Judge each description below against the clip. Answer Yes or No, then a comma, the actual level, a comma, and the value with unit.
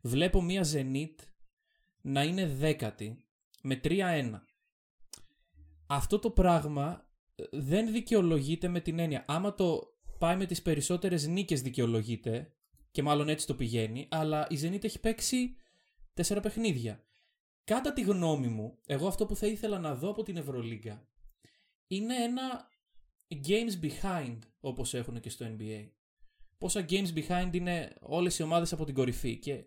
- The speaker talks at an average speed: Yes, average, 140 wpm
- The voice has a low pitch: No, medium, 160 Hz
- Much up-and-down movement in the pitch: Yes, wide, 6.8 semitones